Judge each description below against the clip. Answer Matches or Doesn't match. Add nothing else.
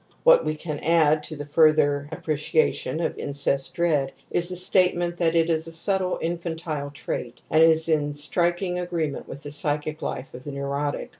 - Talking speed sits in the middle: Matches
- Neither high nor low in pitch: Matches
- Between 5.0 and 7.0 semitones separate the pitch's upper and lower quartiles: Doesn't match